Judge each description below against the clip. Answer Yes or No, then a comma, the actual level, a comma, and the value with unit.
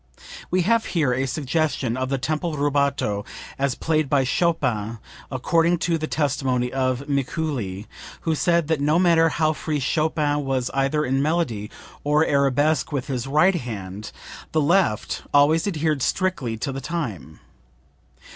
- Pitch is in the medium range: Yes, medium, 145 Hz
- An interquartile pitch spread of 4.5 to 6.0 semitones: No, average, 3.7 semitones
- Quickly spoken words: No, average, 145 wpm